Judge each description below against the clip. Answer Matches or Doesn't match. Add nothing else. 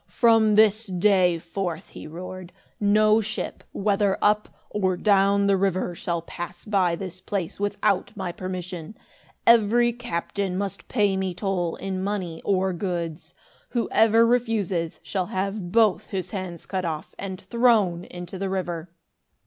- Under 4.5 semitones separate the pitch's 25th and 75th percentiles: Matches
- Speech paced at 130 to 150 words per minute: Matches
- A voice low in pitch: Doesn't match